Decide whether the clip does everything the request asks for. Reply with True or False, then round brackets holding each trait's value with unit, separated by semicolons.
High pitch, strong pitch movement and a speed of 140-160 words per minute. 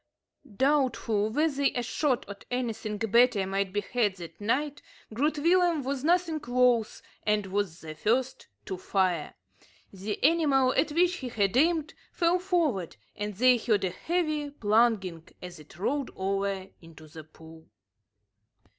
True (235 Hz; 6.9 semitones; 145 wpm)